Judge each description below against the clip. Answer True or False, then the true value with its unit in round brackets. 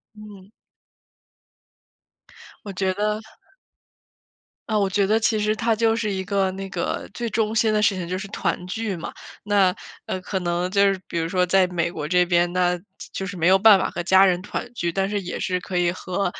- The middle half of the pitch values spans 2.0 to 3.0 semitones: True (2.7 semitones)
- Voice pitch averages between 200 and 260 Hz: False (190 Hz)